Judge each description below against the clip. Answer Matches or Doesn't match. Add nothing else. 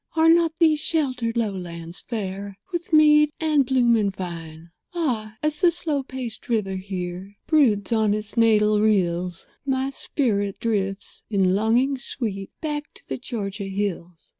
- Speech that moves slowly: Doesn't match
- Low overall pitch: Doesn't match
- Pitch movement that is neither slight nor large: Doesn't match